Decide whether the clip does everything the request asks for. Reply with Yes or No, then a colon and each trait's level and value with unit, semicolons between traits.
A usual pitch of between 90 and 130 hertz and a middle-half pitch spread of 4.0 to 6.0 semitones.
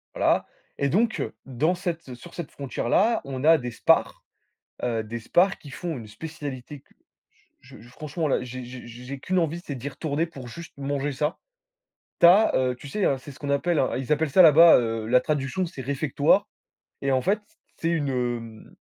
No: medium, 140 Hz; average, 4.5 semitones